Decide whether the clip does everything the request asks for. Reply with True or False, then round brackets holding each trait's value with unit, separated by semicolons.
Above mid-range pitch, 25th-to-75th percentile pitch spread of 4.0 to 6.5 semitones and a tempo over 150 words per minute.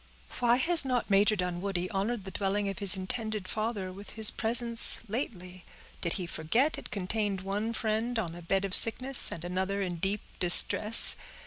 False (200 Hz; 3.5 semitones; 175 wpm)